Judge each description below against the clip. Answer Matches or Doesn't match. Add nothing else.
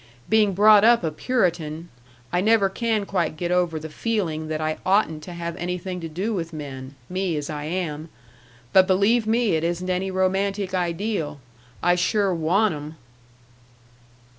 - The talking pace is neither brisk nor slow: Matches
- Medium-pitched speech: Matches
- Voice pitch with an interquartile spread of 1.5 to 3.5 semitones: Doesn't match